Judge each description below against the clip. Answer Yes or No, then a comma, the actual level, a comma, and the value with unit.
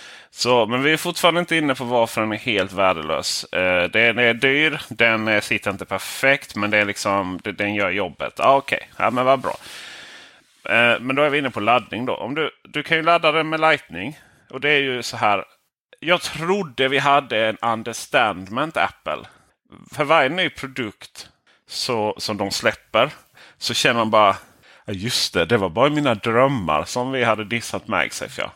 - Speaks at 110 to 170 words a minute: No, average, 185 wpm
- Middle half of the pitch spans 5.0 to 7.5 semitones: Yes, wide, 5.4 semitones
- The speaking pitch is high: No, low, 125 Hz